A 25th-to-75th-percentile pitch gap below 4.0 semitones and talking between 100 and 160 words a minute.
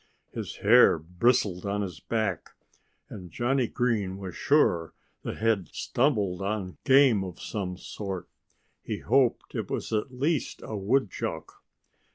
No: average, 4.7 semitones; average, 140 wpm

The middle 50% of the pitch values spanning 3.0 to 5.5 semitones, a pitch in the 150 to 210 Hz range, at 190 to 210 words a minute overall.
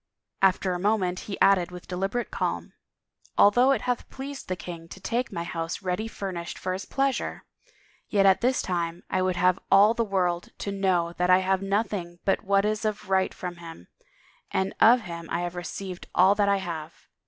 No: narrow, 2.5 semitones; high, 190 Hz; average, 200 wpm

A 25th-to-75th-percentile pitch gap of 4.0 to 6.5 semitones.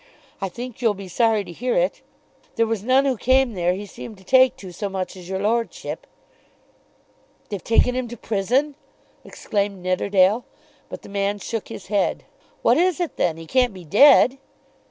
Yes: average, 4.7 semitones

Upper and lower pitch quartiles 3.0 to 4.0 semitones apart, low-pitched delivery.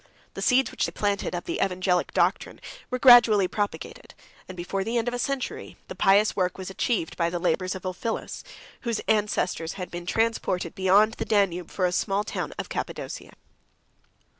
No: average, 3.6 semitones; high, 195 Hz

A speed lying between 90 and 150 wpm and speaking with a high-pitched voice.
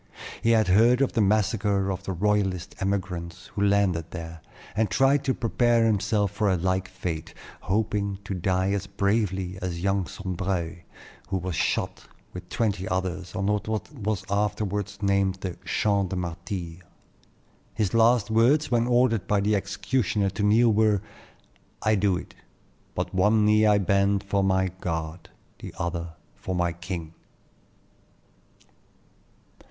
No: average, 145 wpm; low, 100 Hz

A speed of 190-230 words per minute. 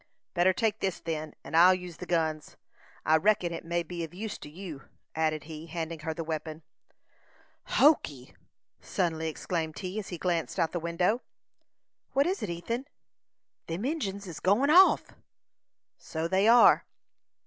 No: average, 160 wpm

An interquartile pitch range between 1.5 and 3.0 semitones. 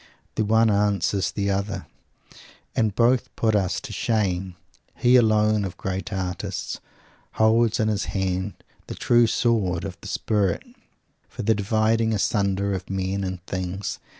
Yes: narrow, 2.5 semitones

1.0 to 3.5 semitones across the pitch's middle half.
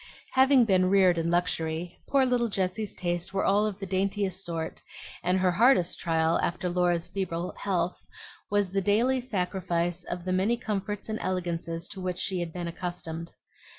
Yes: average, 2.7 semitones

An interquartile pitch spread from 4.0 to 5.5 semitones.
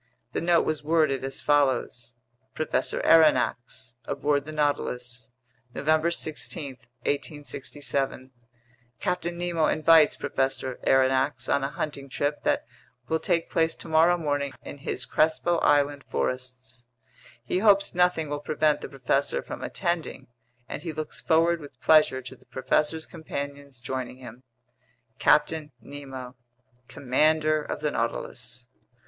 No: average, 3.2 semitones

